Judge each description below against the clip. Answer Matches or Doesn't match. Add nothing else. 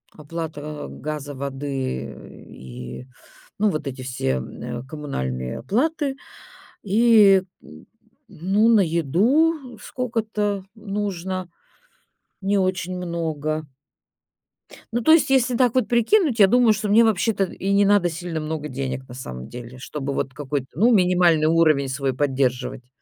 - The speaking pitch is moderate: Matches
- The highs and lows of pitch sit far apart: Matches